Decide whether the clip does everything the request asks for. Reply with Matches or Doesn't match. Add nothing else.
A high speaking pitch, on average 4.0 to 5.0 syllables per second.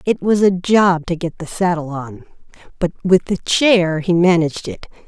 Doesn't match